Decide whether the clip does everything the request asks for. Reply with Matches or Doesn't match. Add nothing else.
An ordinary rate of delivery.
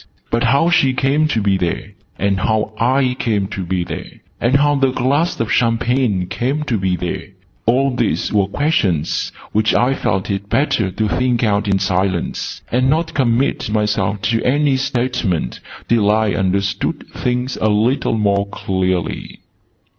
Matches